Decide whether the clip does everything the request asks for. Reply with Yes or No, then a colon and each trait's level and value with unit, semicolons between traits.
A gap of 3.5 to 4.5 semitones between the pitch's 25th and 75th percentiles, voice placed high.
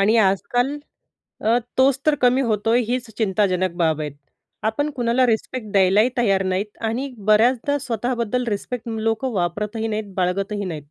Yes: average, 3.9 semitones; high, 220 Hz